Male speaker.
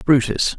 Yes: male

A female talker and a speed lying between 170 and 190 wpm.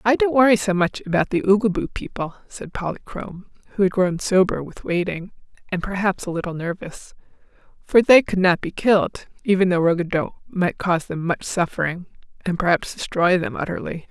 Yes: female; average, 175 wpm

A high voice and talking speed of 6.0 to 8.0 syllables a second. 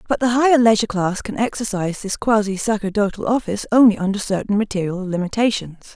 Yes: high, 210 Hz; 6.5 syllables/s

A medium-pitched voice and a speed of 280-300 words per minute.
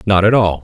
No: low, 100 Hz; fast, 285 wpm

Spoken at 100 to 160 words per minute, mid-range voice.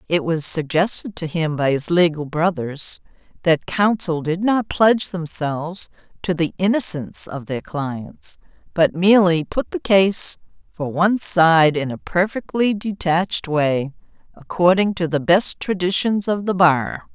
Yes: average, 145 wpm; medium, 175 Hz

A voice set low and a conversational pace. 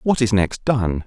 No: low, 110 Hz; fast, 225 wpm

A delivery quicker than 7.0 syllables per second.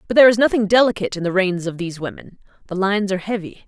Yes: 7.8 syllables/s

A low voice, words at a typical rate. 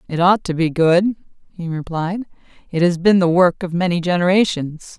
No: medium, 175 Hz; average, 180 wpm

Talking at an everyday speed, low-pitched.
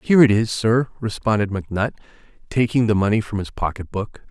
Yes: average, 180 wpm; low, 110 Hz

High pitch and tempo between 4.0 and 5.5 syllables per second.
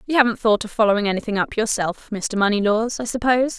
No: high, 220 Hz; 6.4 syllables/s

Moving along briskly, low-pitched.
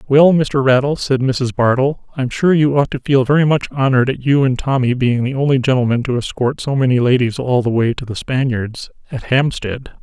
Yes: fast, 215 wpm; low, 130 Hz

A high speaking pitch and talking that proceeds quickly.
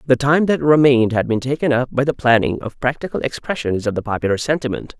No: low, 125 Hz; fast, 215 wpm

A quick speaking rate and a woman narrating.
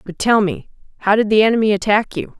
Yes: fast, 225 wpm; female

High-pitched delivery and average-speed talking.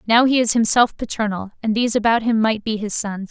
No: high, 220 Hz; fast, 235 wpm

